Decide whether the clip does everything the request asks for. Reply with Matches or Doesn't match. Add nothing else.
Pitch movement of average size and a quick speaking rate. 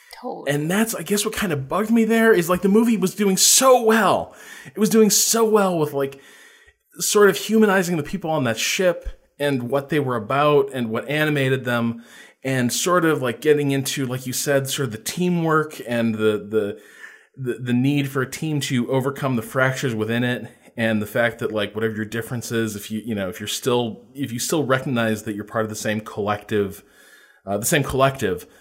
Doesn't match